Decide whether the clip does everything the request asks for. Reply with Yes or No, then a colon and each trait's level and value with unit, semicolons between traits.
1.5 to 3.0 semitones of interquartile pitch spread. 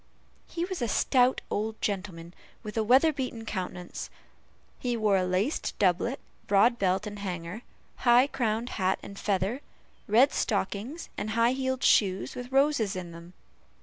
No: average, 4.7 semitones